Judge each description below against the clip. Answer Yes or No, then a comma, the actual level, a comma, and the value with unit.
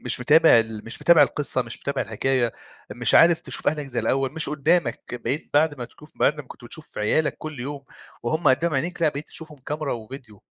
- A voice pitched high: No, medium, 140 Hz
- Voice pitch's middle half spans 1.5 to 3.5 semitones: No, average, 3.9 semitones